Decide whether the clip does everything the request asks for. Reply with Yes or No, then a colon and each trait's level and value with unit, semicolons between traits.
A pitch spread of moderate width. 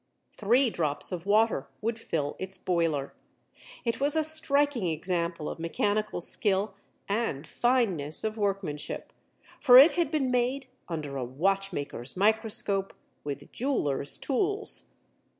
No: wide, 7.0 semitones